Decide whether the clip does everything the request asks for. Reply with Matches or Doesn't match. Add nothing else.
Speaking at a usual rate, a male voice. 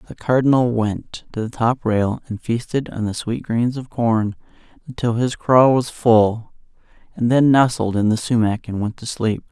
Matches